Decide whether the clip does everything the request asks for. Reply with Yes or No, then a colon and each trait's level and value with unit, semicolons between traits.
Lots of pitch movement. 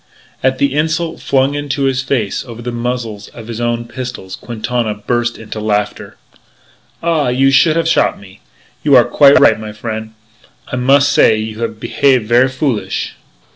No: average, 3.7 semitones